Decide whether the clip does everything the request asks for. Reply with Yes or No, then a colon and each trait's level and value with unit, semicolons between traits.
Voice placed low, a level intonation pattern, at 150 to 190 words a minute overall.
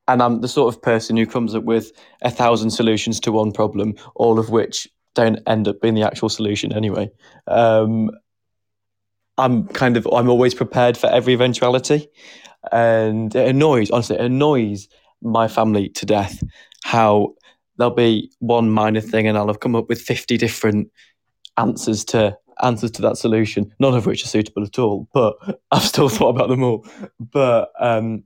Yes: low, 115 Hz; narrow, 2.2 semitones; average, 175 wpm